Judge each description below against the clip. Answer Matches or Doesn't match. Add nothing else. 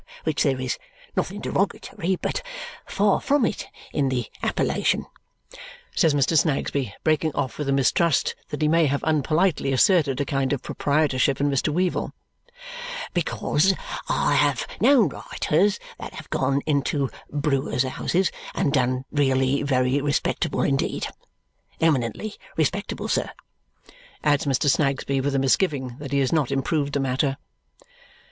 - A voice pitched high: Doesn't match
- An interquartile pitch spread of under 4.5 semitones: Matches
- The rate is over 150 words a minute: Doesn't match